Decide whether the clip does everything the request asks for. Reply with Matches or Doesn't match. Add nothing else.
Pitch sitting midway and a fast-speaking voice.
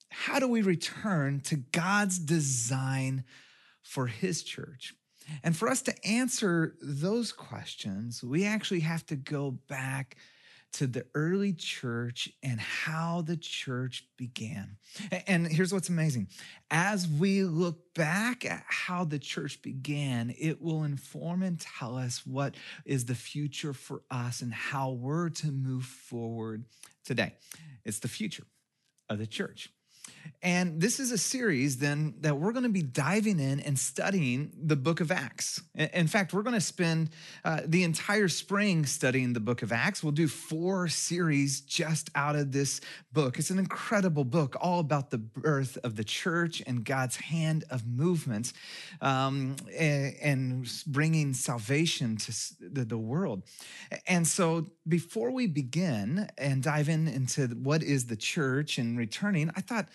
Doesn't match